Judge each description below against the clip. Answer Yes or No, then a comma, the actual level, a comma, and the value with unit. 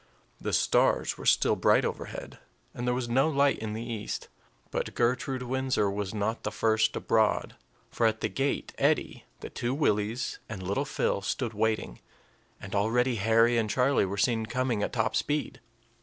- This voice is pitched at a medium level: No, low, 115 Hz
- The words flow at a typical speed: Yes, average, 170 wpm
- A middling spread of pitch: Yes, average, 3.0 semitones